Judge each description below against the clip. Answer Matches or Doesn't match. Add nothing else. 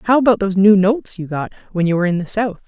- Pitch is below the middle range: Doesn't match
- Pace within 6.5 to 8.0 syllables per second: Matches